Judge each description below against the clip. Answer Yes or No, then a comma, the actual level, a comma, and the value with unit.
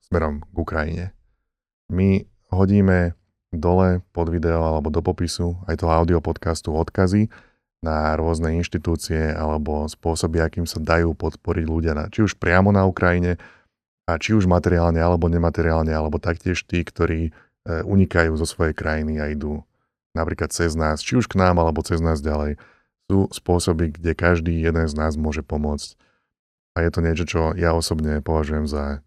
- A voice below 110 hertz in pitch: Yes, very low, 85 Hz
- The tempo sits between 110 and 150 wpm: No, average, 160 wpm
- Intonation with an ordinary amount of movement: No, narrow, 2.0 semitones